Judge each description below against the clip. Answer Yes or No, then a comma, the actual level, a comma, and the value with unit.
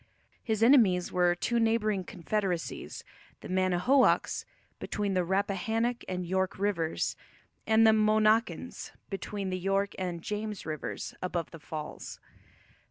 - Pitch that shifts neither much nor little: Yes, average, 3.2 semitones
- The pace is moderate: No, slow, 120 wpm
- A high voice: Yes, high, 195 Hz